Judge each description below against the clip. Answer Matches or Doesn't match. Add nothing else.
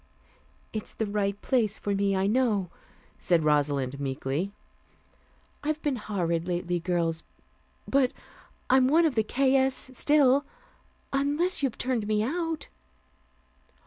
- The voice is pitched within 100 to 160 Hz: Doesn't match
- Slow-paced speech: Matches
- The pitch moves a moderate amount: Doesn't match